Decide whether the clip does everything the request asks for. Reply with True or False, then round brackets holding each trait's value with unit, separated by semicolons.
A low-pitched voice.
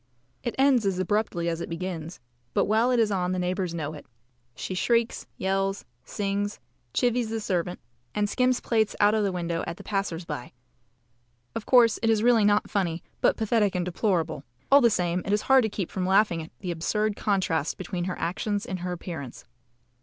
False (195 Hz)